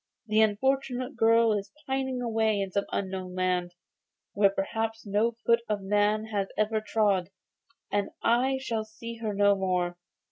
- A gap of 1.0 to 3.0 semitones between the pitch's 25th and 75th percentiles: Yes, narrow, 2.6 semitones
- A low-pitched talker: No, high, 215 Hz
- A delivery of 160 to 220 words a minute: No, average, 150 wpm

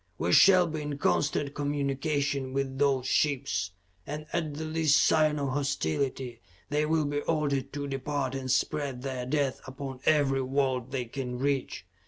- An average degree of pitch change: No, narrow, 2.0 semitones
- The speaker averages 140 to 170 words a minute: Yes, average, 160 wpm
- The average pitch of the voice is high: No, medium, 140 Hz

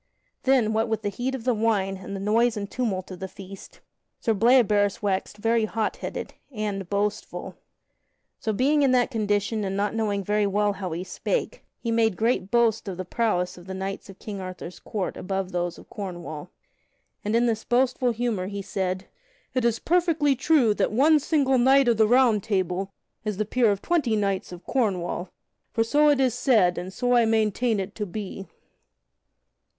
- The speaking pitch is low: No, high, 215 Hz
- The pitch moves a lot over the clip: No, average, 3.8 semitones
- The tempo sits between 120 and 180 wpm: No, average, 190 wpm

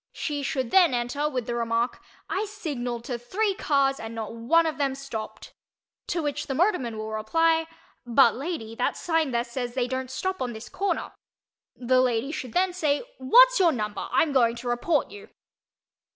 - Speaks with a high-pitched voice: Yes, very high, 260 Hz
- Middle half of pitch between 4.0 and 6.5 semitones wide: Yes, wide, 5.4 semitones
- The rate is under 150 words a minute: No, average, 180 wpm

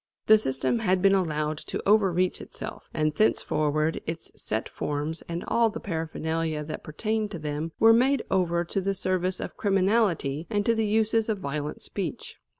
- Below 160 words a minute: No, average, 170 wpm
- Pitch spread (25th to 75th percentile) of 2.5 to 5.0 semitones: No, wide, 5.5 semitones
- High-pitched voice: No, medium, 180 Hz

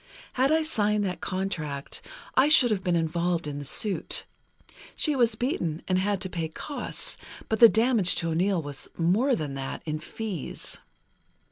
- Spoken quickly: No, average, 165 wpm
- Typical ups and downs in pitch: No, wide, 5.7 semitones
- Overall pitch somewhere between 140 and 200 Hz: Yes, medium, 185 Hz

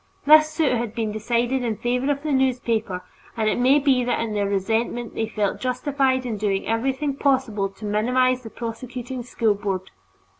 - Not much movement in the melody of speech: No, average, 3.3 semitones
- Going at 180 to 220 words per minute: Yes, average, 185 wpm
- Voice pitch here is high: Yes, high, 240 Hz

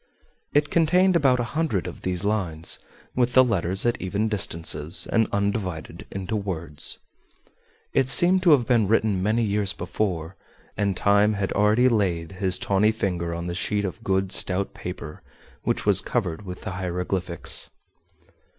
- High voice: No, low, 100 Hz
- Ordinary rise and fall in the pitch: Yes, average, 3.8 semitones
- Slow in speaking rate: No, average, 155 wpm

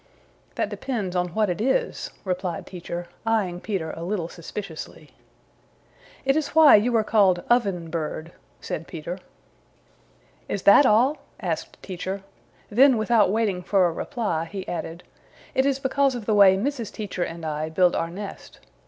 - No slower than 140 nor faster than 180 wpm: Yes, average, 155 wpm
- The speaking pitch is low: No, high, 195 Hz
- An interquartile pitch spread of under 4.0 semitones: No, average, 4.7 semitones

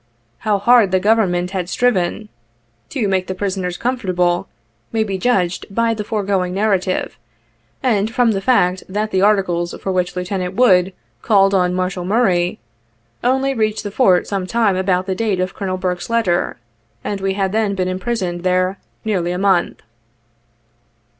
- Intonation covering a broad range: No, average, 2.9 semitones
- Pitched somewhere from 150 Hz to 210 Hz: Yes, high, 190 Hz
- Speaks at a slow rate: No, average, 165 wpm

